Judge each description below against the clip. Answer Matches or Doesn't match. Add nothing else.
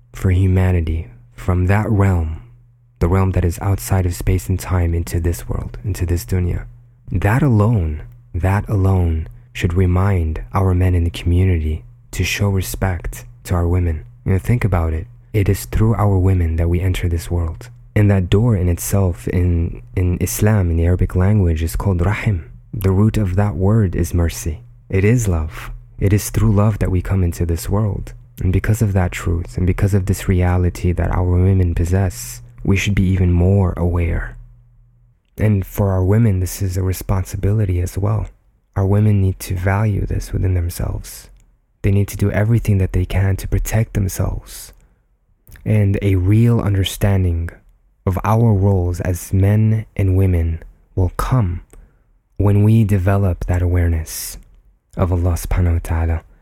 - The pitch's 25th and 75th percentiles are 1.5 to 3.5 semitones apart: Matches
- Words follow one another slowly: Doesn't match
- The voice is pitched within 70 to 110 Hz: Matches